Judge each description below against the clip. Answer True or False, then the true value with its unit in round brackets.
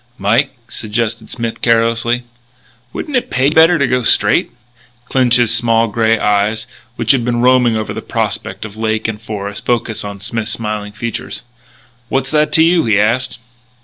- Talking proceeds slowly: False (165 wpm)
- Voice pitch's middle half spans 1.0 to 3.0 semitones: True (2.7 semitones)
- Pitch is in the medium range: False (115 Hz)